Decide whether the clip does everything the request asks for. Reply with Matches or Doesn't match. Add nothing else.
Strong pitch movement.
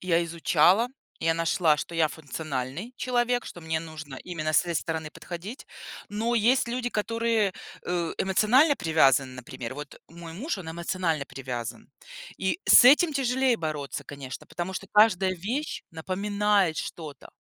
Matches